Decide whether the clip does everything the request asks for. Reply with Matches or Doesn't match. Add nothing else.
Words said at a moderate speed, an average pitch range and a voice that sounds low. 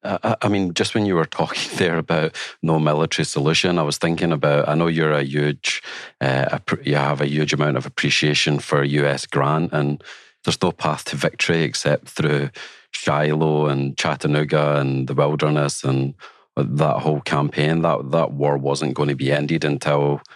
Doesn't match